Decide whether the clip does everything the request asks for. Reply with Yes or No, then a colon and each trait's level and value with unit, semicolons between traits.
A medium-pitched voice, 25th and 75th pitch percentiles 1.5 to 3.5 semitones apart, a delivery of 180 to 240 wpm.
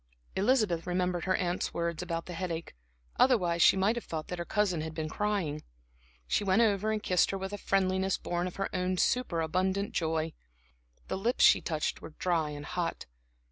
Yes: medium, 180 Hz; average, 2.8 semitones; average, 185 wpm